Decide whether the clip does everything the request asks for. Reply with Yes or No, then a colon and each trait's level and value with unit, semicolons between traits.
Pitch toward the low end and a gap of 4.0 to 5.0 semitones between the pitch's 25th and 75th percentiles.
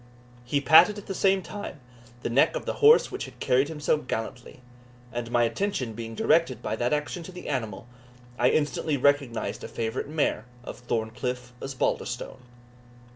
Yes: low, 130 Hz; average, 4.6 semitones